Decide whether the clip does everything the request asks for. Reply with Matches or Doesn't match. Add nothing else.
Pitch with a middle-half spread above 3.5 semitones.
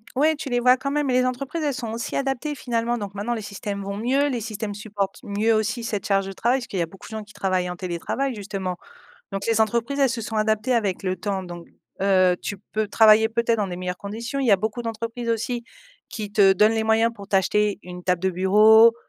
Doesn't match